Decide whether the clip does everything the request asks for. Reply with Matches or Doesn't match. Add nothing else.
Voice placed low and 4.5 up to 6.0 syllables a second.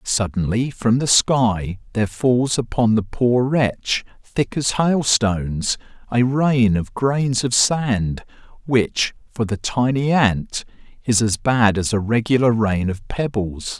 Doesn't match